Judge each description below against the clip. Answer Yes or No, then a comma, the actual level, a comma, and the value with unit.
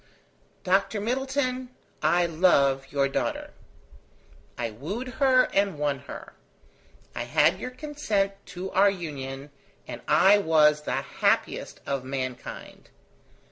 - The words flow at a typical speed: No, slow, 115 wpm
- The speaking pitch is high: No, medium, 180 Hz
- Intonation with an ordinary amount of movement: No, wide, 7.3 semitones